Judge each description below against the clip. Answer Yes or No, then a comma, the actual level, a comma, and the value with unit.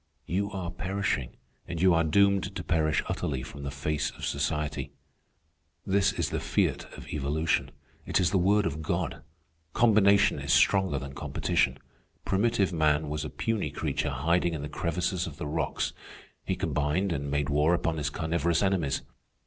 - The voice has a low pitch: Yes, very low, 85 Hz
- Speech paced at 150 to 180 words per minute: Yes, average, 165 wpm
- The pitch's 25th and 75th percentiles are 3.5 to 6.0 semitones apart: Yes, average, 4.5 semitones